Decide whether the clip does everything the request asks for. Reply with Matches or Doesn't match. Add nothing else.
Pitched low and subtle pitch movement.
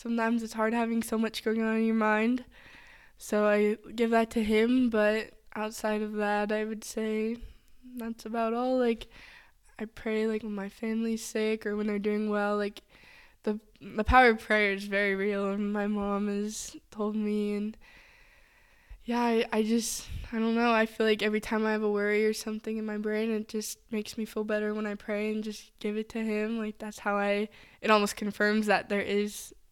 Doesn't match